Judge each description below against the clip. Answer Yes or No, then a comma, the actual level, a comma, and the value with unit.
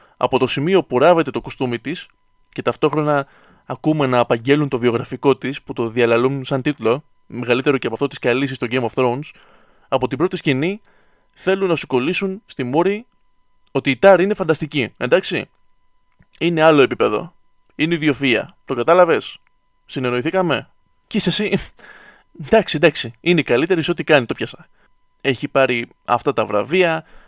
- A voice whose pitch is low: No, medium, 145 Hz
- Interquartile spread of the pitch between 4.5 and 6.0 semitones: Yes, wide, 5.6 semitones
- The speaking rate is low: No, average, 160 wpm